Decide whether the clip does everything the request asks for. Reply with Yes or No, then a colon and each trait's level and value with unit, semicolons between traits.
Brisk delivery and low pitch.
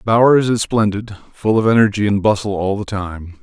No: average, 195 wpm; low, 105 Hz